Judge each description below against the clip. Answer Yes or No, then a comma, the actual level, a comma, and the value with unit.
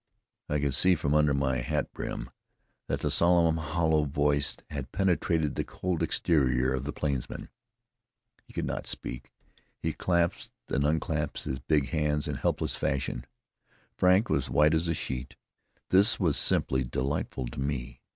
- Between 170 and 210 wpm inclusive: No, average, 160 wpm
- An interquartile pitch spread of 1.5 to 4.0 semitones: Yes, average, 3.6 semitones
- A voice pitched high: No, very low, 75 Hz